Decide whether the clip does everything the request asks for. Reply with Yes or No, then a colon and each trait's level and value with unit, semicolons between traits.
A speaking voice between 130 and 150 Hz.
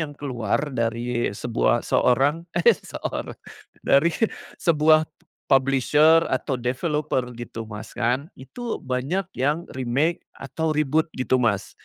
Yes: low, 135 Hz